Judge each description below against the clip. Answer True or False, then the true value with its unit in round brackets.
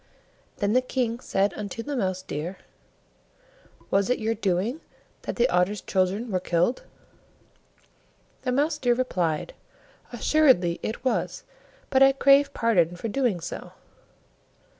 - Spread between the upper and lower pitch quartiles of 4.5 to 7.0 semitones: True (5.6 semitones)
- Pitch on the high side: True (225 Hz)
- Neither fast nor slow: False (130 wpm)